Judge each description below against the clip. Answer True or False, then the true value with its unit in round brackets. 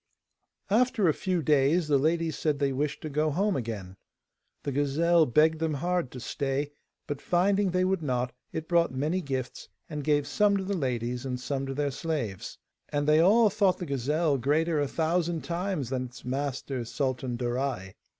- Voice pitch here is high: False (150 Hz)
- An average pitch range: True (4.4 semitones)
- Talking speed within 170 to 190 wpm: True (180 wpm)